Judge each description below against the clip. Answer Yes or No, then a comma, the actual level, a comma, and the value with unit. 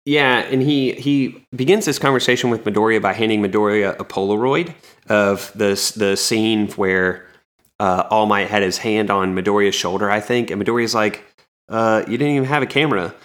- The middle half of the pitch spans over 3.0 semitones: Yes, average, 3.7 semitones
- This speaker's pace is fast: No, average, 180 wpm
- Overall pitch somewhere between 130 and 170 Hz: No, low, 110 Hz